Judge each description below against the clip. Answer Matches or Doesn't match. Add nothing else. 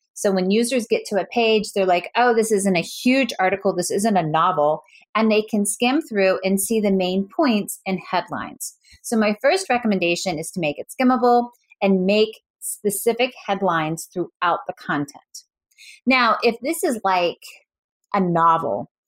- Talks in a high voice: Matches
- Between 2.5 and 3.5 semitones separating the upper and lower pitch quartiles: Doesn't match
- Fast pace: Doesn't match